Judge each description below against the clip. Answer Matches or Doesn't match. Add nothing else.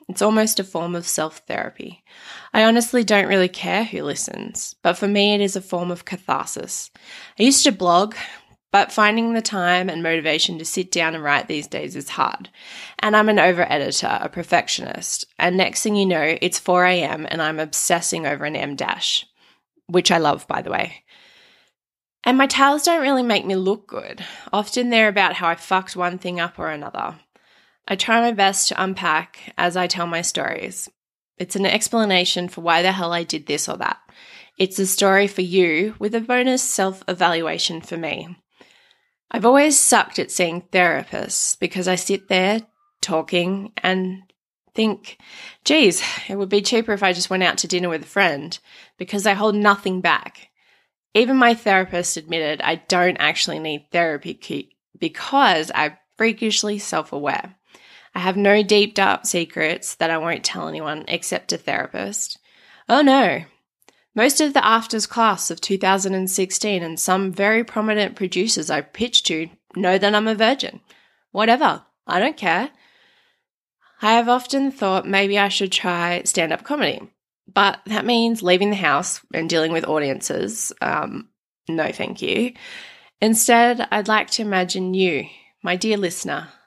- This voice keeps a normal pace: Matches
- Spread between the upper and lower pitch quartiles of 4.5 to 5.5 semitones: Doesn't match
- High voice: Matches